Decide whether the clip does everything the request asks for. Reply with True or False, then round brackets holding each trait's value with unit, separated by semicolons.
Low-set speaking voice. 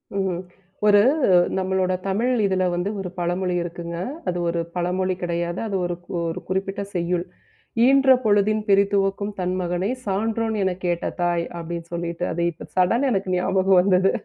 False (185 Hz)